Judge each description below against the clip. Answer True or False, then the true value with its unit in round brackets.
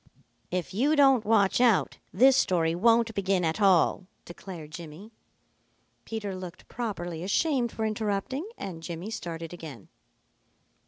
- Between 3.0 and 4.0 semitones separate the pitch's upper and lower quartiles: False (4.7 semitones)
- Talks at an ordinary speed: False (125 wpm)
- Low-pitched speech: False (195 Hz)